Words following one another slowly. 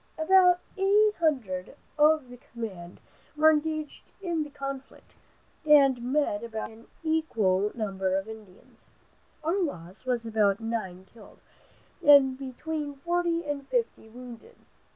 Yes: slow, 125 wpm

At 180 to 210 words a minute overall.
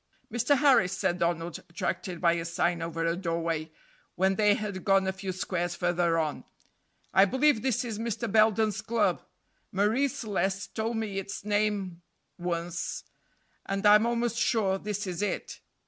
No: average, 155 wpm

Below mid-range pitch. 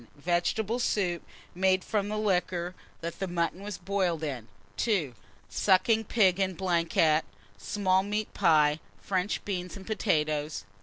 No: medium, 185 Hz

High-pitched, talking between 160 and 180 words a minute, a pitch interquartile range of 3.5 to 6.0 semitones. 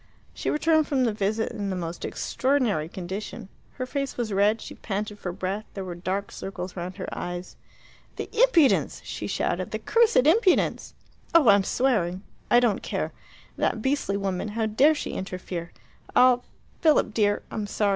Yes: high, 210 Hz; average, 165 wpm; average, 5.3 semitones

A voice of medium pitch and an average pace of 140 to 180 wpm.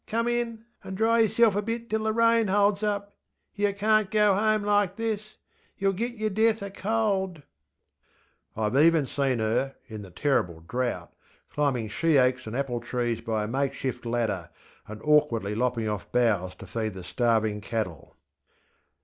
Yes: medium, 145 Hz; average, 165 wpm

